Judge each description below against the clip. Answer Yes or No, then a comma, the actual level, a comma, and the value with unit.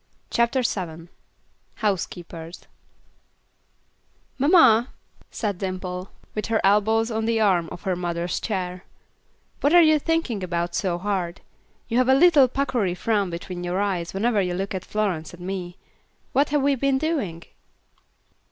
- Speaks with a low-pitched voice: No, high, 200 Hz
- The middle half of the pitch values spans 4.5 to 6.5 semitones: Yes, average, 5.2 semitones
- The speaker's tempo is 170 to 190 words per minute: No, average, 145 wpm